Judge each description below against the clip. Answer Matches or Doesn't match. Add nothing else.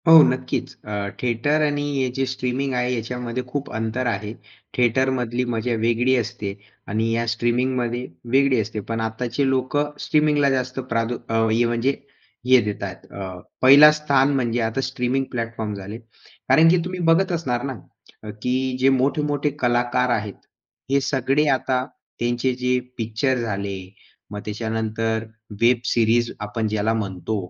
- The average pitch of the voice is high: Doesn't match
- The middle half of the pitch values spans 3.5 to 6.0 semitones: Doesn't match